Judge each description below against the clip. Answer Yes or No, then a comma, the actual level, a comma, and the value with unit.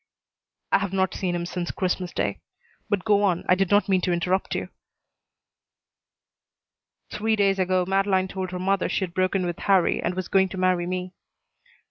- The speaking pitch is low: No, medium, 185 Hz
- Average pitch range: No, narrow, 1.3 semitones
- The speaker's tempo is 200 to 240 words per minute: No, average, 175 wpm